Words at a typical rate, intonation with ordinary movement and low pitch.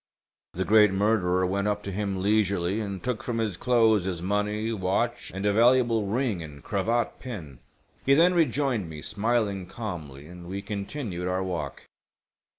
Yes: average, 160 wpm; average, 3.6 semitones; low, 100 Hz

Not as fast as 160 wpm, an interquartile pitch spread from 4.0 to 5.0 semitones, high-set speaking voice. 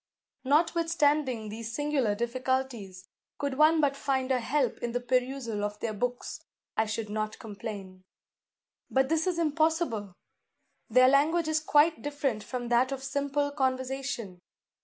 Yes: average, 140 wpm; average, 4.3 semitones; very high, 260 Hz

